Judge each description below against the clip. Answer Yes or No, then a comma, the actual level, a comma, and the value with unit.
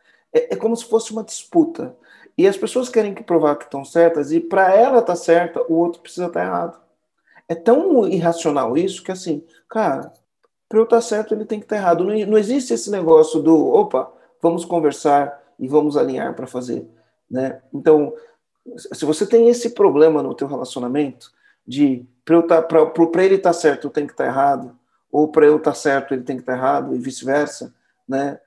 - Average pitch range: No, wide, 6.6 semitones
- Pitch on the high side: No, medium, 170 Hz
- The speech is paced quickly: Yes, fast, 200 wpm